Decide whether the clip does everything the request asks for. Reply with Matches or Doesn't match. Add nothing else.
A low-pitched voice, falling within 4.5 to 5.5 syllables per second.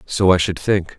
Matches